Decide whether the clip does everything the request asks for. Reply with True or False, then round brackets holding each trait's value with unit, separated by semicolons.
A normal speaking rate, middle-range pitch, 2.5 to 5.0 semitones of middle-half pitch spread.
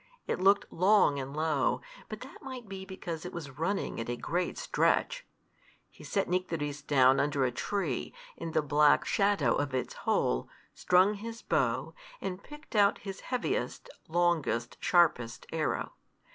False (155 wpm; 170 Hz; 5.6 semitones)